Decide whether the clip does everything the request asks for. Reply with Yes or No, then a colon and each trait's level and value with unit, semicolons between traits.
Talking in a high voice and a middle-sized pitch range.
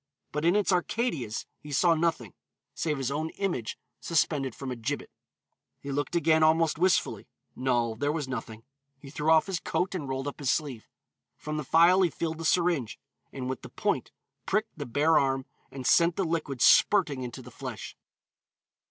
No: medium, 150 Hz; average, 4.1 semitones